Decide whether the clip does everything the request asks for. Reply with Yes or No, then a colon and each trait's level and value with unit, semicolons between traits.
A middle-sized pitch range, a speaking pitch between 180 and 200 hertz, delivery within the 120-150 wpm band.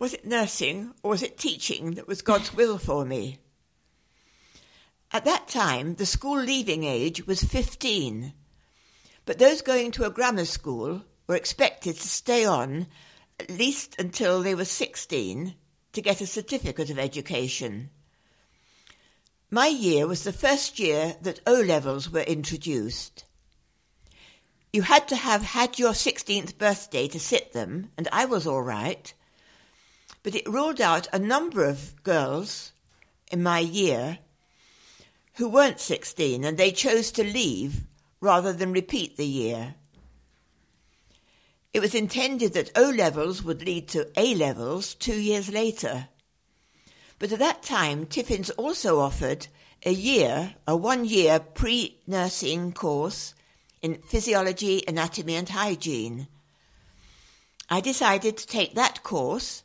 No: wide, 6.7 semitones; medium, 185 Hz; average, 140 wpm